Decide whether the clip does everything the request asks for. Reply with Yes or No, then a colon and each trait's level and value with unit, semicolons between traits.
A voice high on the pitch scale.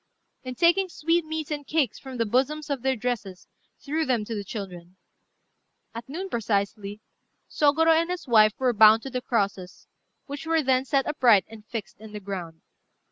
Yes: high, 245 Hz